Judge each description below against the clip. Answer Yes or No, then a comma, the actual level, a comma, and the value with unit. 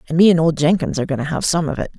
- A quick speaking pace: Yes, fast, 360 wpm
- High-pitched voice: No, medium, 160 Hz